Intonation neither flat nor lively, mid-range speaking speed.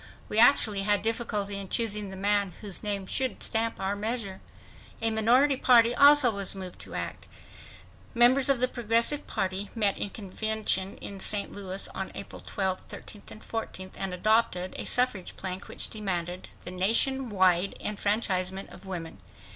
Yes: average, 3.2 semitones; average, 160 wpm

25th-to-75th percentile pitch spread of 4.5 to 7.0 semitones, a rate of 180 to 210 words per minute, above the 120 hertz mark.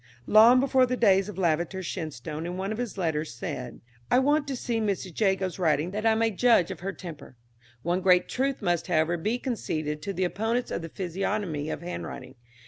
Yes: average, 5.2 semitones; average, 200 wpm; high, 190 Hz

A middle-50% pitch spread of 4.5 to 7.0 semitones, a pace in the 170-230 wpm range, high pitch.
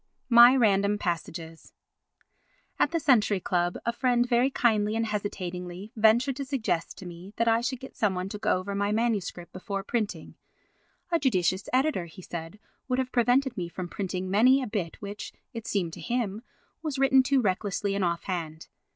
Yes: average, 4.8 semitones; average, 175 wpm; high, 210 Hz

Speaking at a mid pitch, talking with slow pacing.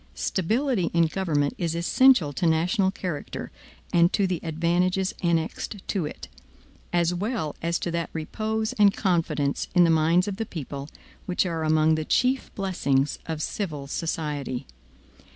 No: medium, 170 Hz; average, 150 wpm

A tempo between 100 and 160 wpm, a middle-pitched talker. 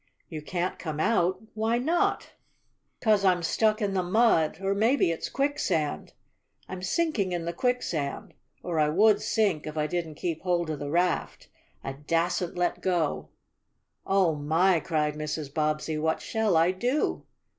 Yes: average, 155 wpm; medium, 175 Hz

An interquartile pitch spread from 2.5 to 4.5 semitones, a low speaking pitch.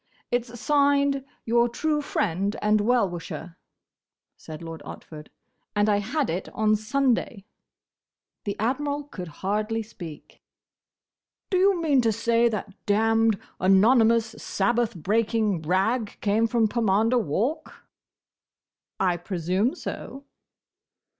No: average, 3.8 semitones; high, 220 Hz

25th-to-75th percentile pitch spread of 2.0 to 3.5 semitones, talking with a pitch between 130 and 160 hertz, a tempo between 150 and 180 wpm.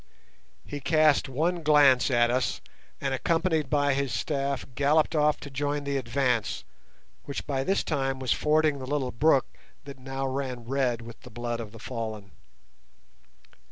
Yes: average, 2.8 semitones; low, 135 Hz; average, 155 wpm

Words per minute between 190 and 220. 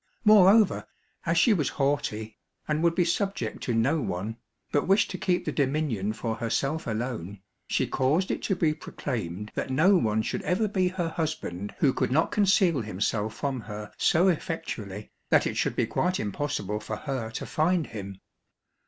No: average, 175 wpm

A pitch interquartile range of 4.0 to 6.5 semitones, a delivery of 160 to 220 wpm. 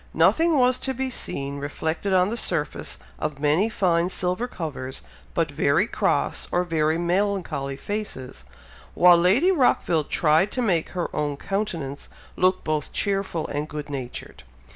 No: average, 5.2 semitones; average, 145 wpm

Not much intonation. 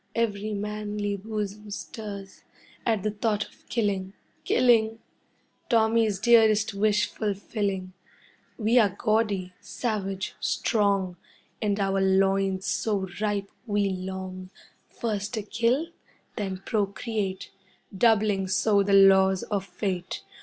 Yes: narrow, 2.1 semitones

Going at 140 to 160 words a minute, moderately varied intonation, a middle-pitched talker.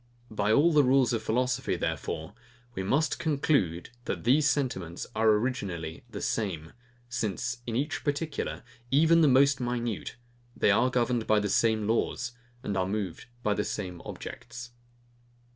No: average, 150 wpm; average, 4.5 semitones; low, 120 Hz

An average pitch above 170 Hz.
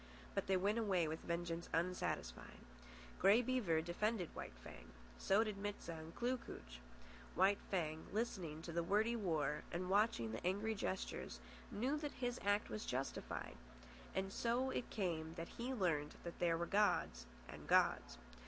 Yes: medium, 185 Hz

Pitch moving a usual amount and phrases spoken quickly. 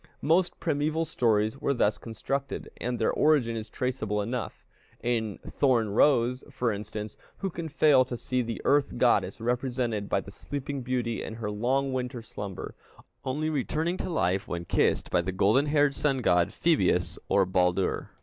No: average, 4.7 semitones; average, 165 wpm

